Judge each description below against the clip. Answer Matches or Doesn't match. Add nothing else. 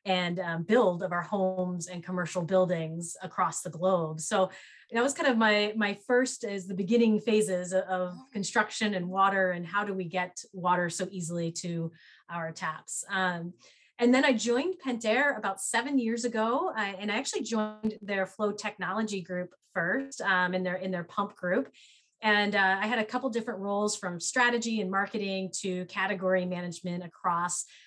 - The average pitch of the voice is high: Matches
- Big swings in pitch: Doesn't match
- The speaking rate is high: Doesn't match